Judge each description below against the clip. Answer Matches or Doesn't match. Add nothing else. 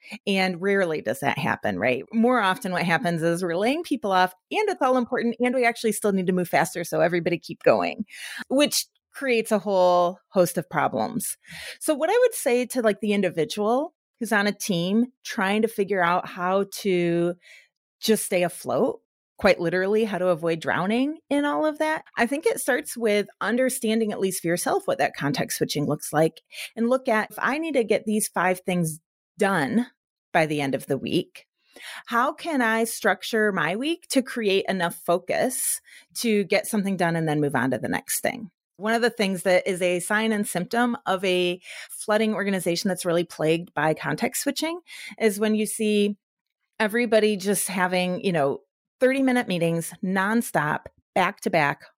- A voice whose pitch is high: Matches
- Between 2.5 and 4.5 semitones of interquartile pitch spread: Doesn't match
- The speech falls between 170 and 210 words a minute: Matches